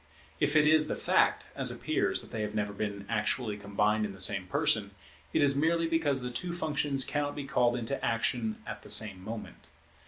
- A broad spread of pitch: Yes, wide, 5.8 semitones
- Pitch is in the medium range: No, low, 120 Hz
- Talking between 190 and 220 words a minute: Yes, average, 200 wpm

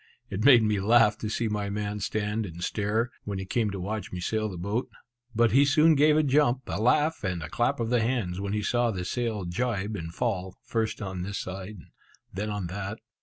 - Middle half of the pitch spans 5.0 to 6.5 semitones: No, average, 3.7 semitones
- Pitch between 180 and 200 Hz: No, low, 105 Hz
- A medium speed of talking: No, fast, 220 wpm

